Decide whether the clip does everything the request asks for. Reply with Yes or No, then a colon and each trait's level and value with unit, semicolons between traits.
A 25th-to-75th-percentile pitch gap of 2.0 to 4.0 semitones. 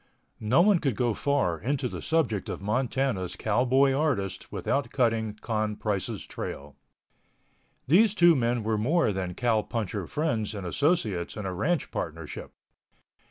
No: wide, 5.4 semitones